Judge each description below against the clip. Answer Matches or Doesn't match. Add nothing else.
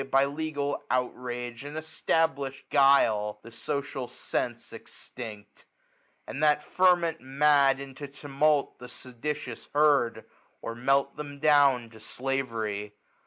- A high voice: Doesn't match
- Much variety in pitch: Doesn't match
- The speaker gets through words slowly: Matches